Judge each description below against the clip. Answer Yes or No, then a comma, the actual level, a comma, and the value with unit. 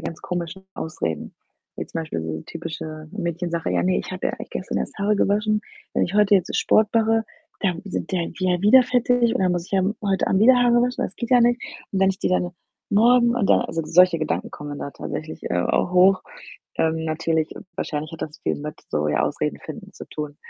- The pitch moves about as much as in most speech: Yes, average, 4.9 semitones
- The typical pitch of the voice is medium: Yes, medium, 180 Hz